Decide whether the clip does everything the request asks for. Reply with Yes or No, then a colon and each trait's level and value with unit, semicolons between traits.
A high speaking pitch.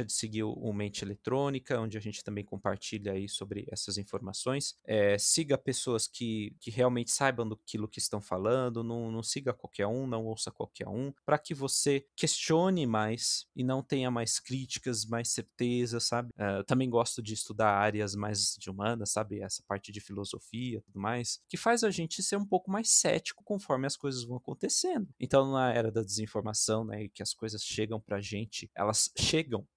No: low, 115 Hz